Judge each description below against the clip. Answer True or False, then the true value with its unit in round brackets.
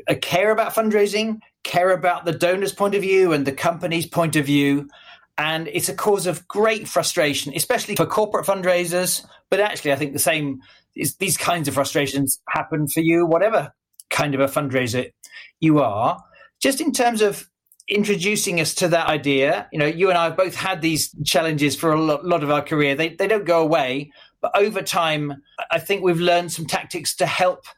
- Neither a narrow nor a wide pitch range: True (4.4 semitones)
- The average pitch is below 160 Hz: False (170 Hz)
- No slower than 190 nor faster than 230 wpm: True (195 wpm)